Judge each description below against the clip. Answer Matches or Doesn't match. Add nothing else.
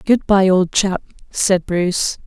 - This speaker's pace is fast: Doesn't match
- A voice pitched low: Doesn't match